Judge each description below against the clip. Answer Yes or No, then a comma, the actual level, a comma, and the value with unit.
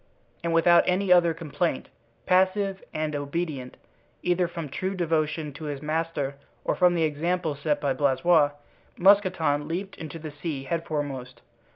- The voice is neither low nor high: Yes, medium, 160 Hz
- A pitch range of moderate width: Yes, average, 3.3 semitones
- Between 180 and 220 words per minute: No, average, 145 wpm